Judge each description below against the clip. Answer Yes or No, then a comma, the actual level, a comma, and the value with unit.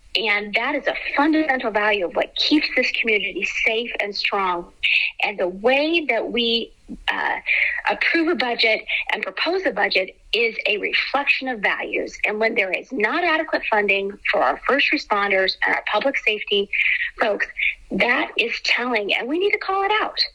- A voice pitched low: No, very high, 260 Hz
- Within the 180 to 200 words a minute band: No, average, 170 wpm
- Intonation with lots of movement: Yes, wide, 8.0 semitones